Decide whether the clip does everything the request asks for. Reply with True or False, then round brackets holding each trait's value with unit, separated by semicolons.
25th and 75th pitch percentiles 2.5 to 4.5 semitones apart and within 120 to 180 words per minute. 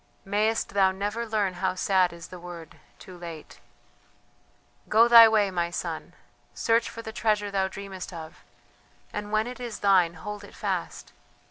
True (3.4 semitones; 160 wpm)